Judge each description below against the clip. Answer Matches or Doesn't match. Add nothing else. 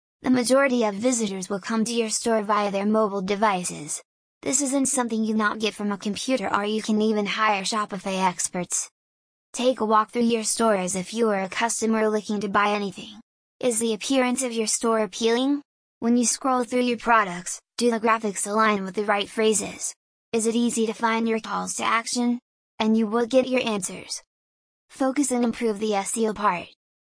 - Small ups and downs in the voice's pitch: Matches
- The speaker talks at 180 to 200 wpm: Matches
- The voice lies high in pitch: Matches